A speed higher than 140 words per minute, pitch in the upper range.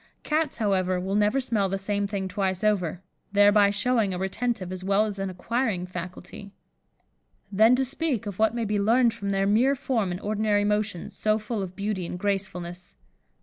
Yes: average, 185 wpm; high, 205 Hz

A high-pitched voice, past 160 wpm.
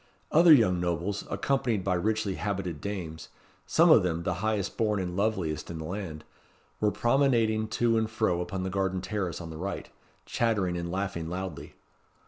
No: very low, 95 Hz; average, 170 wpm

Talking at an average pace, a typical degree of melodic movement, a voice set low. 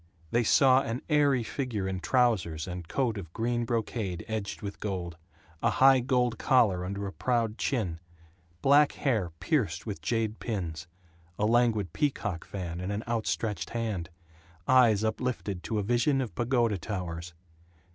Yes: average, 155 wpm; average, 4.7 semitones; low, 110 Hz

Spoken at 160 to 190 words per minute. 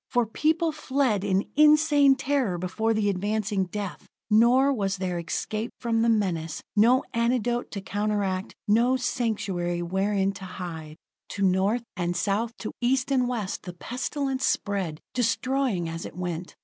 No: average, 150 wpm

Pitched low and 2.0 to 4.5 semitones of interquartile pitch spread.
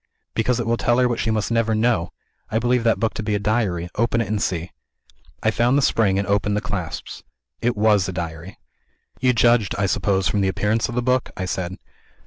Yes: low, 110 Hz; average, 3.3 semitones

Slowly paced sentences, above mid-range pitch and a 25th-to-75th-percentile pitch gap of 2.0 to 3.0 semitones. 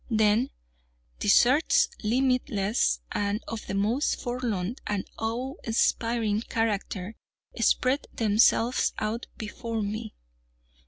Yes: slow, 95 wpm; high, 225 Hz; narrow, 2.6 semitones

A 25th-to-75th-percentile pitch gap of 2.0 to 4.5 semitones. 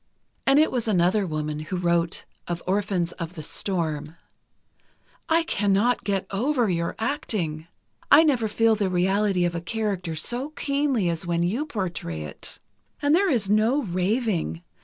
No: wide, 5.6 semitones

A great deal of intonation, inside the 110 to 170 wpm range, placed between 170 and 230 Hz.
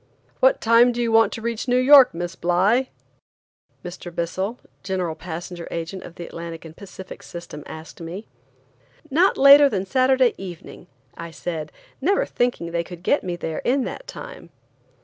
Yes: wide, 6.5 semitones; average, 165 wpm; high, 190 Hz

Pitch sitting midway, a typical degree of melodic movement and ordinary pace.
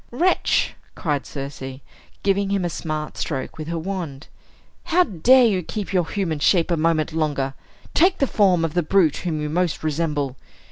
Yes: medium, 165 Hz; average, 4.4 semitones; average, 175 wpm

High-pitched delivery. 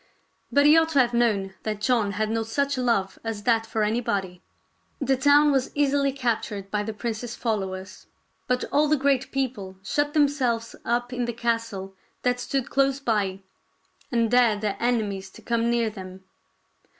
Yes: high, 235 Hz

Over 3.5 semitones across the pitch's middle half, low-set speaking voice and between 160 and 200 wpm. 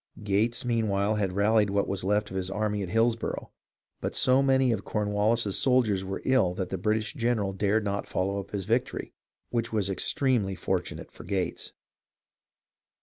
No: average, 2.8 semitones; low, 105 Hz; average, 170 wpm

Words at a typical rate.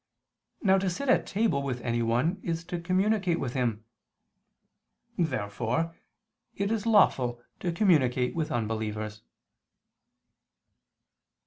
No: slow, 105 wpm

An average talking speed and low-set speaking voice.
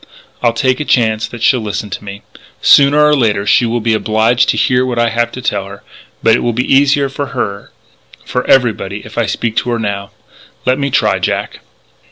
No: fast, 215 wpm; low, 120 Hz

